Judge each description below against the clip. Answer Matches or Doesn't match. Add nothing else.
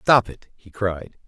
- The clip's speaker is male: Matches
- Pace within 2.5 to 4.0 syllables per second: Matches